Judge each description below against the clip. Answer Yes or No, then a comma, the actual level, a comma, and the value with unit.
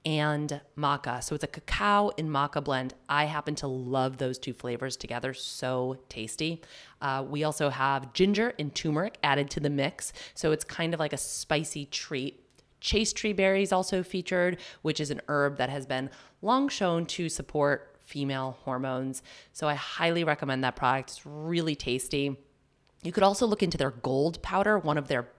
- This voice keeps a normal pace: Yes, average, 180 wpm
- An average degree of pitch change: Yes, average, 3.9 semitones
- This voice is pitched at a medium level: Yes, medium, 145 Hz